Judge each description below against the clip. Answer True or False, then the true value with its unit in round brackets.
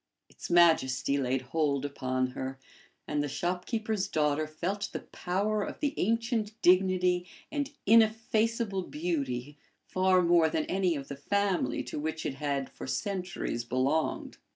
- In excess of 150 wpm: False (140 wpm)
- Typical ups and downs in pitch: False (6.1 semitones)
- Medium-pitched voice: True (175 Hz)